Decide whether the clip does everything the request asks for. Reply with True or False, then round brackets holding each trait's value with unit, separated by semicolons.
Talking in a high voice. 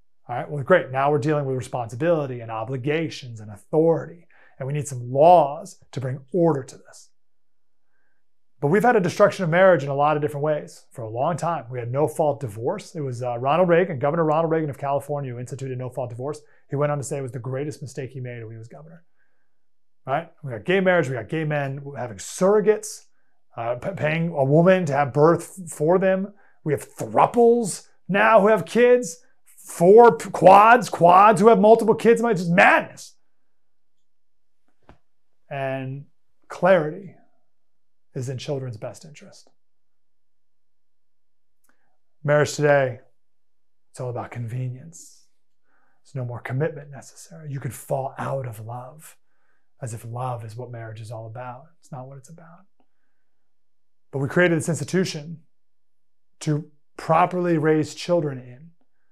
False (140 Hz)